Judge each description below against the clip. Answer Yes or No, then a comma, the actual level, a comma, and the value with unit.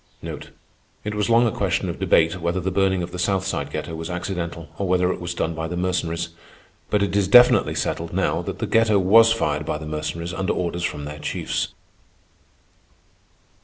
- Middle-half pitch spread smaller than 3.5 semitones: Yes, average, 3.0 semitones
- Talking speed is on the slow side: No, average, 195 wpm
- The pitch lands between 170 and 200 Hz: No, very low, 90 Hz